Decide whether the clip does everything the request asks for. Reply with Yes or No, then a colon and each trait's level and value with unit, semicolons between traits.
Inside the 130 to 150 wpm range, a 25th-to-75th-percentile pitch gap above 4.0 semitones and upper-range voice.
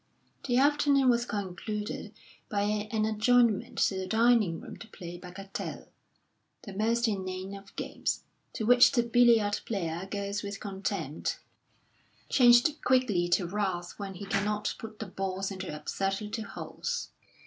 No: average, 140 wpm; average, 3.4 semitones; high, 205 Hz